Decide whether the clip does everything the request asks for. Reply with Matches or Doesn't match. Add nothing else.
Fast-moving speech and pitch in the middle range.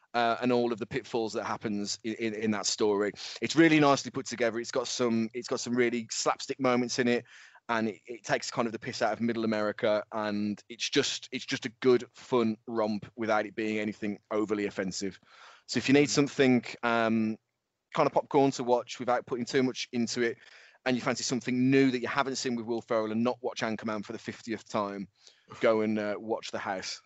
Doesn't match